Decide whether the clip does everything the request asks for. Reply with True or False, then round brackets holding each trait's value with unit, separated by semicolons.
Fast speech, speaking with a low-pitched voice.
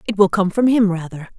False (260 wpm; 195 Hz)